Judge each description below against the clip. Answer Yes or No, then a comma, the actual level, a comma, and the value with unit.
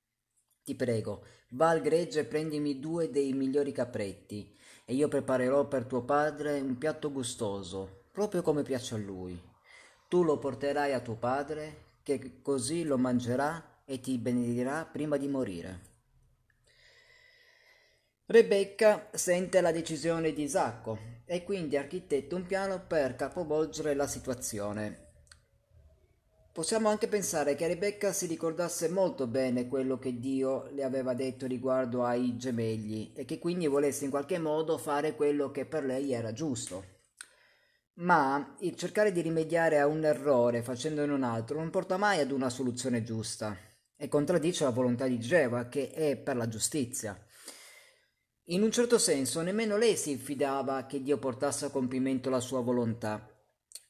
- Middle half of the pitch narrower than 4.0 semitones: No, average, 4.6 semitones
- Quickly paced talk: No, average, 150 wpm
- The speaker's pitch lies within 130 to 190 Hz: Yes, medium, 140 Hz